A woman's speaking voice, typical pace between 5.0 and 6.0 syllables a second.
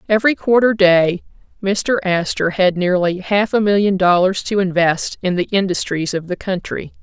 Yes: female; 5.6 syllables/s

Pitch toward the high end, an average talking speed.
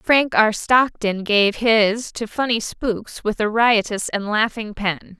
Yes: high, 220 Hz; average, 160 wpm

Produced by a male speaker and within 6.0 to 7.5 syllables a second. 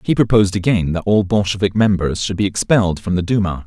Yes: male; 6.2 syllables/s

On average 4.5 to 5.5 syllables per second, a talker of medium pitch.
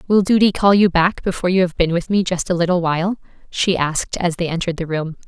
No: 6.3 syllables/s; medium, 180 Hz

